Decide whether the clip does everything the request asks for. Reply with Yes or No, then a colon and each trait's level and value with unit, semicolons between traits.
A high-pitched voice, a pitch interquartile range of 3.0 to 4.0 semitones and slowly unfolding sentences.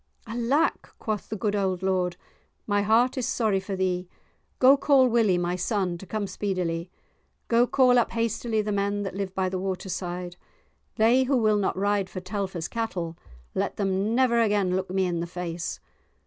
No: high, 200 Hz; average, 3.5 semitones; average, 175 wpm